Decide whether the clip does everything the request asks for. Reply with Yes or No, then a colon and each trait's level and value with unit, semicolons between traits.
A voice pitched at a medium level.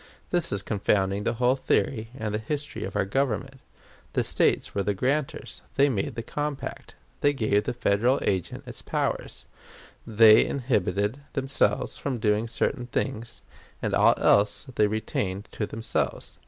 No: low, 110 Hz